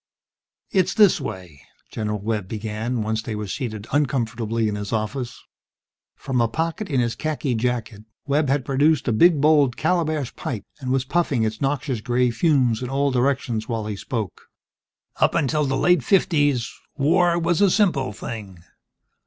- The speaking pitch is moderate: No, low, 130 Hz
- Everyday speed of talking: Yes, average, 160 wpm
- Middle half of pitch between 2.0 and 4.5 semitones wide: No, average, 5.2 semitones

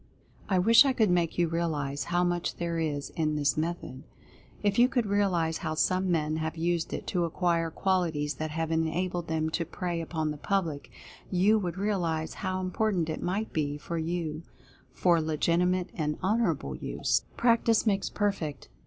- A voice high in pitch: No, medium, 170 Hz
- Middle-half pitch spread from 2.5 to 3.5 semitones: Yes, average, 2.9 semitones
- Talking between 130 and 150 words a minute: No, average, 170 wpm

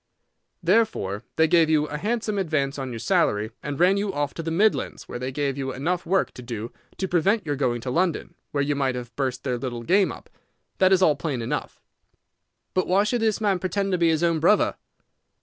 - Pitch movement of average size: No, wide, 6.2 semitones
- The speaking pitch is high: No, medium, 155 Hz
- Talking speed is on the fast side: Yes, fast, 220 wpm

